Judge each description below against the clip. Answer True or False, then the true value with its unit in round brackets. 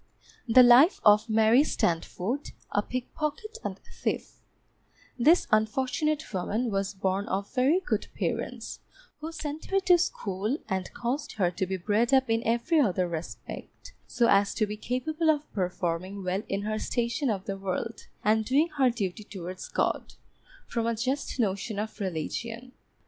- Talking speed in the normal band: True (155 wpm)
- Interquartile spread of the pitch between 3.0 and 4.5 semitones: False (5.2 semitones)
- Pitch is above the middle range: True (225 Hz)